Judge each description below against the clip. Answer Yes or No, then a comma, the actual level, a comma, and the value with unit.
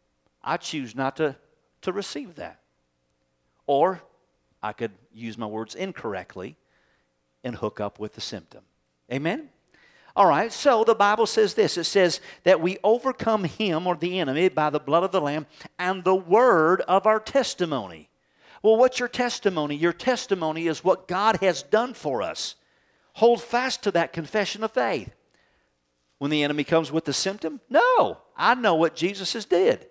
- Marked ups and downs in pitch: Yes, wide, 7.7 semitones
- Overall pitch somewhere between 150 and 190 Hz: Yes, medium, 175 Hz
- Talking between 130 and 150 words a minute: No, average, 165 wpm